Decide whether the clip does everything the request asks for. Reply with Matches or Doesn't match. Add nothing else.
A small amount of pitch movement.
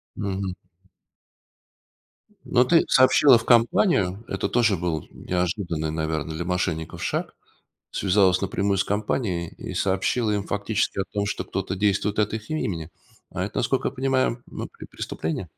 Doesn't match